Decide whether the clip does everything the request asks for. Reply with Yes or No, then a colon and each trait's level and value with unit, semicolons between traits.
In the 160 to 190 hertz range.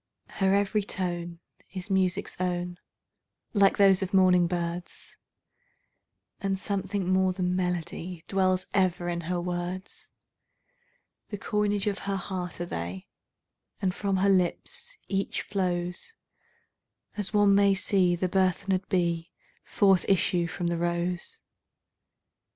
Yes: medium, 185 Hz